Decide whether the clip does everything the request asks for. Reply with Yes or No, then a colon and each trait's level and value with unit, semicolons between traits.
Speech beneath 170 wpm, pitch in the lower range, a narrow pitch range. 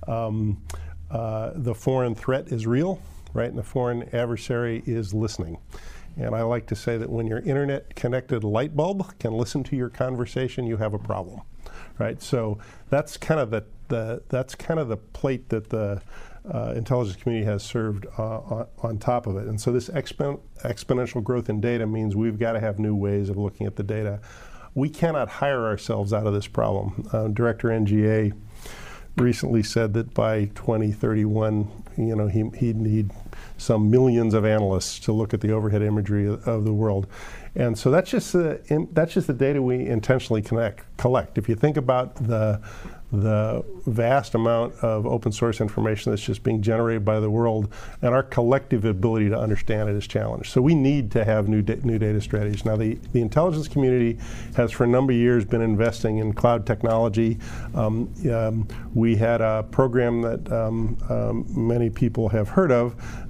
No: average, 185 wpm; low, 115 Hz; narrow, 2.2 semitones